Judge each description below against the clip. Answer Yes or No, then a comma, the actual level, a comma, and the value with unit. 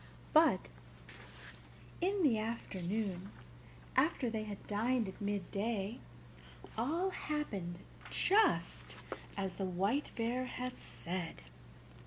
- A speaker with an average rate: No, slow, 95 wpm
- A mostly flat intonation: No, average, 4.8 semitones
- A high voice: Yes, high, 220 Hz